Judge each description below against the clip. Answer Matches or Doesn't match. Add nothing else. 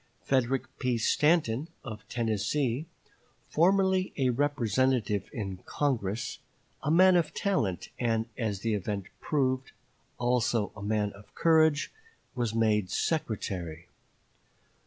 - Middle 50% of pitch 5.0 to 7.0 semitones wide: Matches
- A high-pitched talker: Doesn't match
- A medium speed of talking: Doesn't match